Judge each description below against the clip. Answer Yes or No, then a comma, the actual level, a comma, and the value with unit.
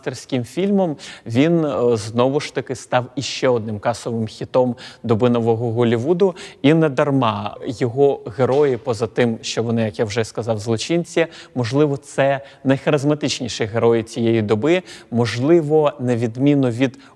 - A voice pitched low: Yes, low, 130 Hz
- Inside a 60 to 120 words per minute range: No, average, 130 wpm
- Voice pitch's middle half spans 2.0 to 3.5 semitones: No, average, 4.1 semitones